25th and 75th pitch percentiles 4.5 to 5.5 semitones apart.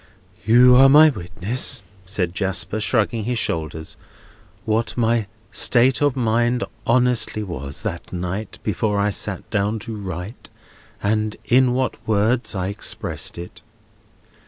No: average, 3.9 semitones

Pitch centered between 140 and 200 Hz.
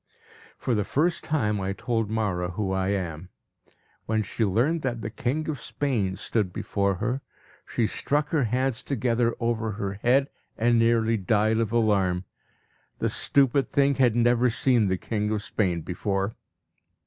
No: low, 110 Hz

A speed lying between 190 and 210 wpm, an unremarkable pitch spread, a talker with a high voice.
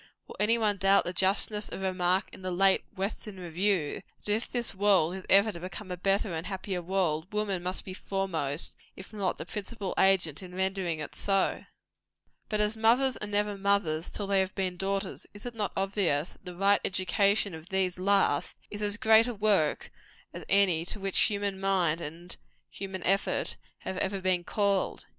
No: average, 195 wpm; narrow, 2.1 semitones; high, 195 Hz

